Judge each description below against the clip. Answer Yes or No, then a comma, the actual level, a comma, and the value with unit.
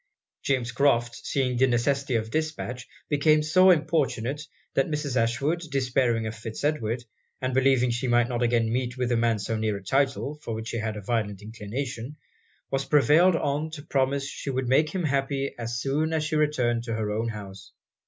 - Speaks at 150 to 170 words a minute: No, average, 190 wpm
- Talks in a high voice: No, low, 130 Hz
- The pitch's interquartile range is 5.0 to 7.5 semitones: No, average, 3.8 semitones